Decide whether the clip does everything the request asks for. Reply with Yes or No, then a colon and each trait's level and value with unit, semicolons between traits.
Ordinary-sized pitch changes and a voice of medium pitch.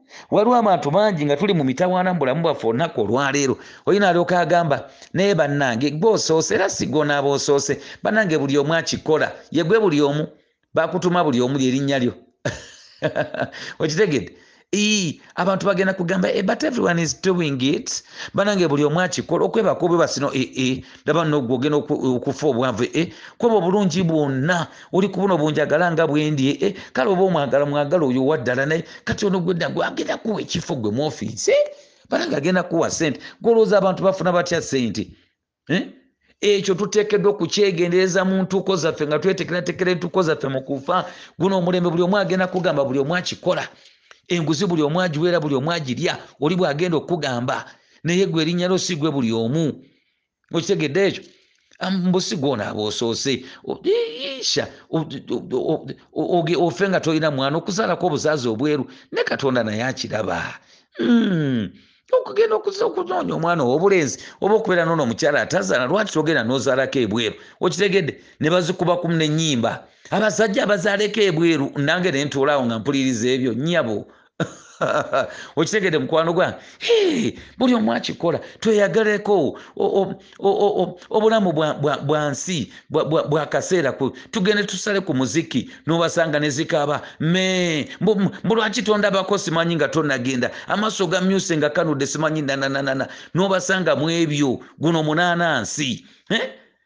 Yes: average, 5.0 semitones; medium, 170 Hz